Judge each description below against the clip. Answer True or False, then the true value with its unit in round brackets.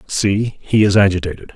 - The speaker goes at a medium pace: True (155 wpm)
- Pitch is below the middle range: True (100 Hz)